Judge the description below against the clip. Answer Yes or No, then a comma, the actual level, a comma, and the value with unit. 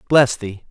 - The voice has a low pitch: Yes, low, 115 Hz